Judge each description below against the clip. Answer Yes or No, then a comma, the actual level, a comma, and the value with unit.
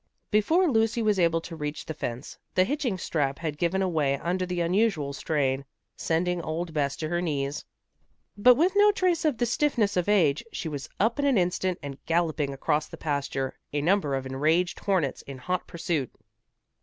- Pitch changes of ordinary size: No, wide, 5.8 semitones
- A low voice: No, medium, 170 Hz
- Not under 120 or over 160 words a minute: No, average, 185 wpm